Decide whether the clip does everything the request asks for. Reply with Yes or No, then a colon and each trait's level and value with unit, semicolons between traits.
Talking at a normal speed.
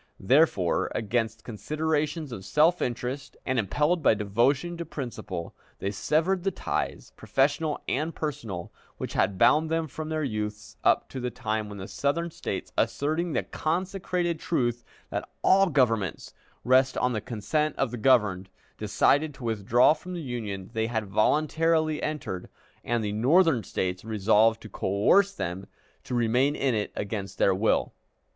Yes: average, 155 wpm